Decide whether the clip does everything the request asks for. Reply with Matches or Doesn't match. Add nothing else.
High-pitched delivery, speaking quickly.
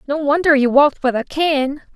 Matches